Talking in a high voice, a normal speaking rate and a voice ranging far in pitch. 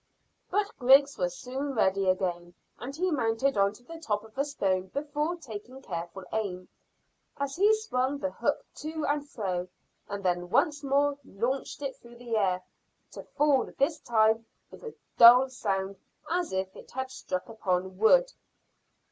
Yes: high, 245 Hz; average, 165 wpm; wide, 6.7 semitones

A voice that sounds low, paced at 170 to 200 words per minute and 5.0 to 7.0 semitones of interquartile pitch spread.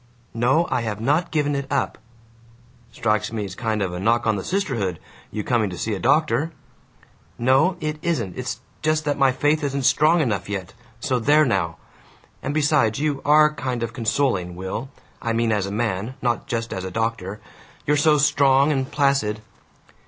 Yes: low, 125 Hz; average, 180 wpm; average, 5.3 semitones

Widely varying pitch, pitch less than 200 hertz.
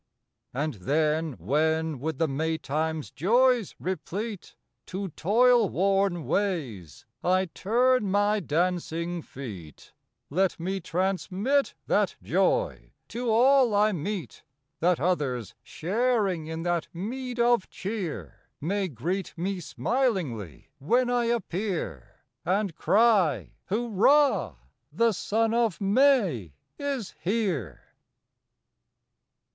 Yes: wide, 6.0 semitones; medium, 185 Hz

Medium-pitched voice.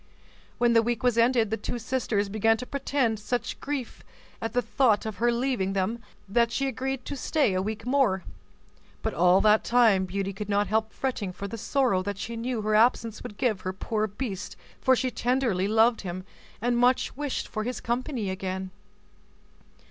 No: high, 225 Hz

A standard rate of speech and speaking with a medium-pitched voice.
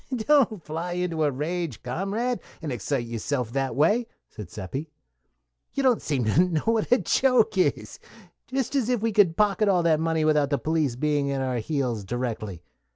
Yes: average, 180 wpm; medium, 155 Hz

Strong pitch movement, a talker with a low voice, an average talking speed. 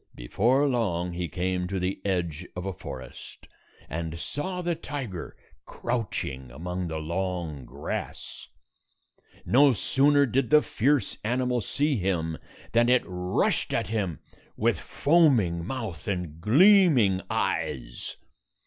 No: wide, 7.2 semitones; very low, 95 Hz; slow, 120 wpm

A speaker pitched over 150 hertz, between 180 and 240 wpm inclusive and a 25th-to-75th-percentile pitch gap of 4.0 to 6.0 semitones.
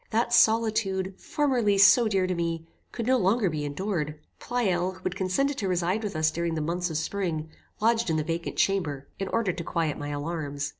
Yes: medium, 185 Hz; average, 200 wpm; average, 4.8 semitones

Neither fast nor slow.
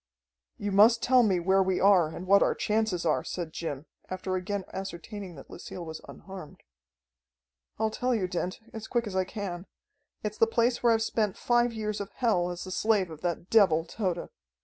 Yes: average, 195 wpm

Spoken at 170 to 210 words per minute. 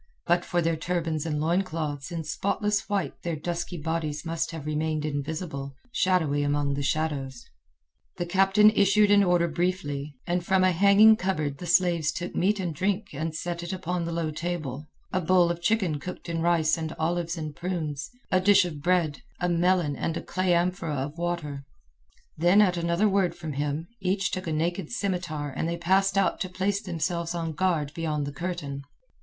Yes: average, 185 wpm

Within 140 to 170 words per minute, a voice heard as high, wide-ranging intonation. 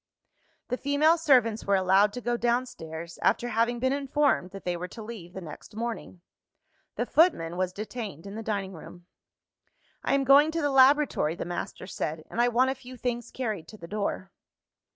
No: average, 190 wpm; high, 225 Hz; wide, 5.7 semitones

